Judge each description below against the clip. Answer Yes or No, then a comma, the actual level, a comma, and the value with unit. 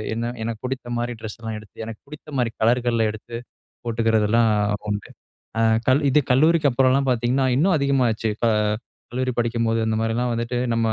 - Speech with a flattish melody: Yes, narrow, 2.3 semitones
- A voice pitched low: Yes, low, 120 Hz